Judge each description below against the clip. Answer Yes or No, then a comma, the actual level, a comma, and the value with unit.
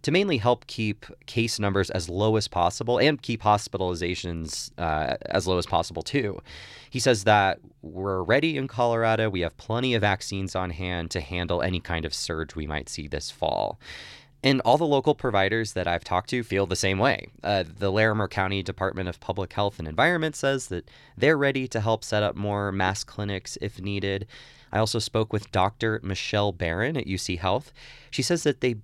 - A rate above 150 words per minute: Yes, average, 195 wpm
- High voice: No, low, 100 Hz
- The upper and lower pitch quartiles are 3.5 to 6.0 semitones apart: Yes, average, 4.4 semitones